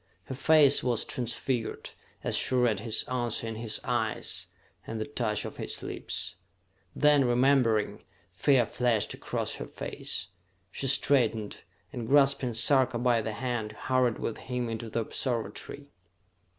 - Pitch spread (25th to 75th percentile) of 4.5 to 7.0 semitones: No, average, 2.7 semitones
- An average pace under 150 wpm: Yes, average, 140 wpm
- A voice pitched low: Yes, low, 120 Hz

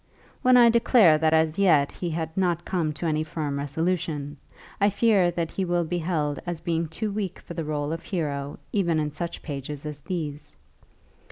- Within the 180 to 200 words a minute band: Yes, average, 190 wpm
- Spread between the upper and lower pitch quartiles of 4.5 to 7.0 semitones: No, average, 3.1 semitones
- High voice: No, medium, 165 Hz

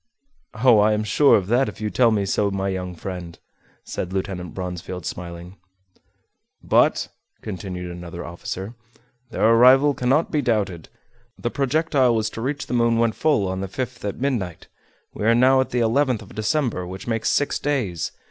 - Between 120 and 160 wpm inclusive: No, average, 175 wpm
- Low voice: Yes, low, 110 Hz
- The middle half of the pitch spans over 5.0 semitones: Yes, wide, 5.4 semitones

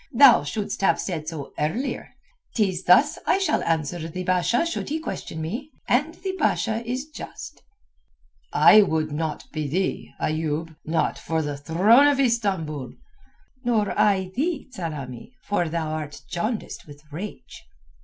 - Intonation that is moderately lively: No, wide, 7.4 semitones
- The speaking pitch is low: No, medium, 185 Hz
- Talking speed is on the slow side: No, average, 145 wpm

